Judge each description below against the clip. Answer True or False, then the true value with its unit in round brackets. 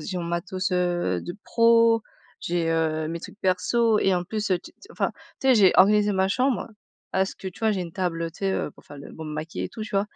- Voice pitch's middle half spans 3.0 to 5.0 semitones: True (3.8 semitones)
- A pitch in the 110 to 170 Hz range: False (185 Hz)